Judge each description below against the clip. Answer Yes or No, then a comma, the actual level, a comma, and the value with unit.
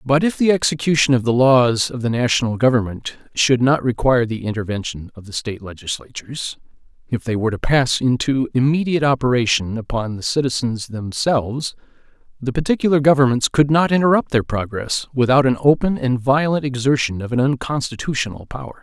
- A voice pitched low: Yes, low, 130 Hz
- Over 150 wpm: Yes, average, 160 wpm